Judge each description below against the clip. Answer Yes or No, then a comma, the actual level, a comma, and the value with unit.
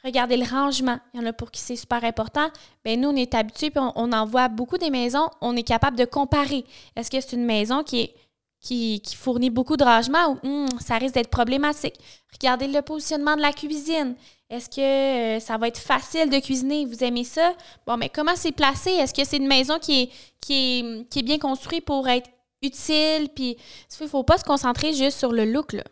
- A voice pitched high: Yes, very high, 265 Hz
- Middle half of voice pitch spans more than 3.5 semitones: No, average, 3.2 semitones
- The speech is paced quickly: Yes, fast, 225 wpm